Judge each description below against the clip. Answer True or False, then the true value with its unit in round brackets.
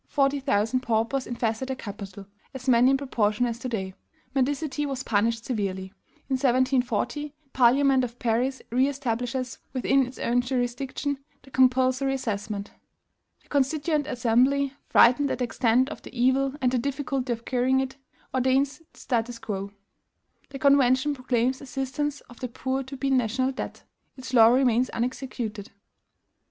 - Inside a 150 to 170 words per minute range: True (155 wpm)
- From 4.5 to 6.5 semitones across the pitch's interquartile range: False (2.4 semitones)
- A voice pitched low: False (255 Hz)